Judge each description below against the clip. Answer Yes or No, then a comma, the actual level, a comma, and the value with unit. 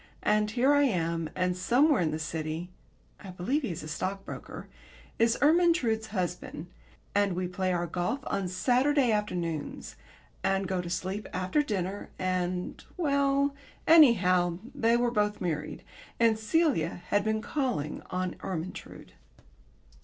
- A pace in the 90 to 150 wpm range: Yes, average, 140 wpm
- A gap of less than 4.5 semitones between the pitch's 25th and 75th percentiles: No, wide, 5.4 semitones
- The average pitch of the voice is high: Yes, high, 195 Hz